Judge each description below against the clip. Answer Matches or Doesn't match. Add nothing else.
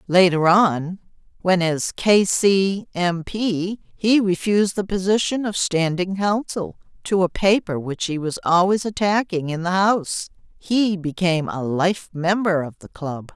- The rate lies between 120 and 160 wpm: Matches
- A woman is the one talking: Matches